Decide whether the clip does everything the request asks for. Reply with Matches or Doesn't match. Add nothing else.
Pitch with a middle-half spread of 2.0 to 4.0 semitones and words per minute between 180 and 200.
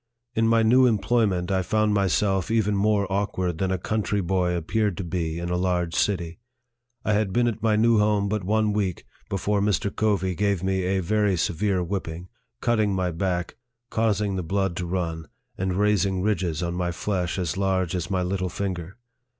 Matches